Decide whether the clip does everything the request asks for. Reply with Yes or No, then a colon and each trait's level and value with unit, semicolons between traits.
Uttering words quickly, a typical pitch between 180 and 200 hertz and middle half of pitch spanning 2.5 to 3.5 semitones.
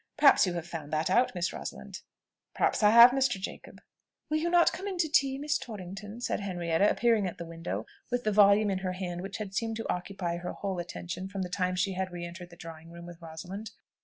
No: fast, 230 wpm; high, 190 Hz; average, 4.3 semitones